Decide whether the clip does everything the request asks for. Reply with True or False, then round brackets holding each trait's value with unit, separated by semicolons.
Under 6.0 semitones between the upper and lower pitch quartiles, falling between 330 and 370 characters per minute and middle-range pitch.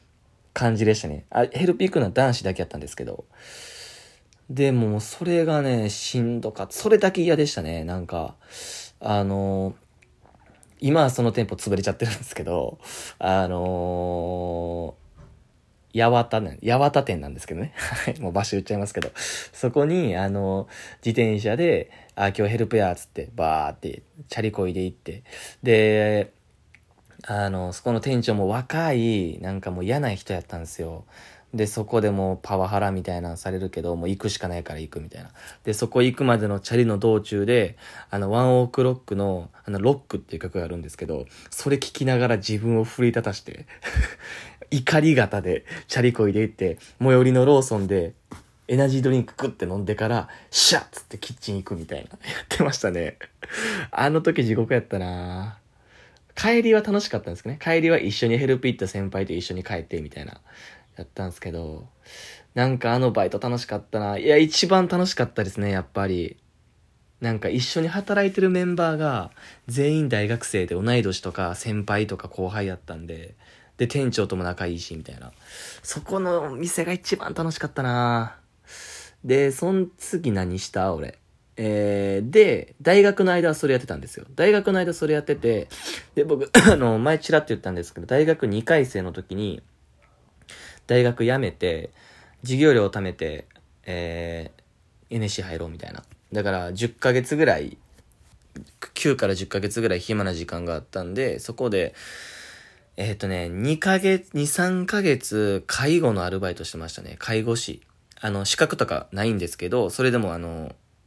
False (5.4 semitones; 340 characters per minute; 110 Hz)